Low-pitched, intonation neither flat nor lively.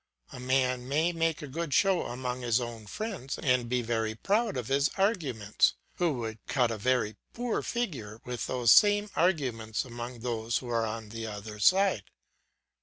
No: low, 125 Hz; wide, 6.3 semitones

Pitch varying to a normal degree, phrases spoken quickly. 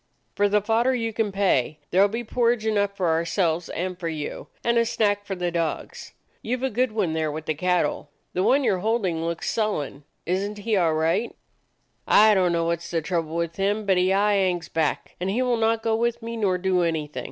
Yes: average, 4.7 semitones; fast, 230 wpm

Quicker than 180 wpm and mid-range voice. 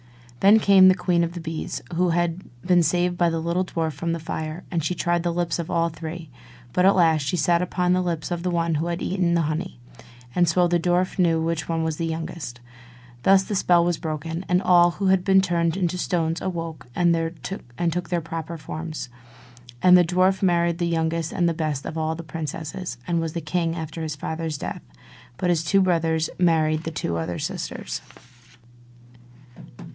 Yes: average, 195 wpm; medium, 170 Hz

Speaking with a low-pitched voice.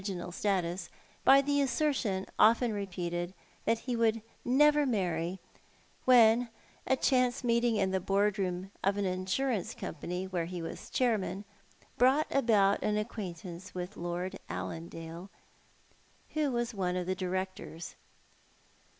No: high, 195 Hz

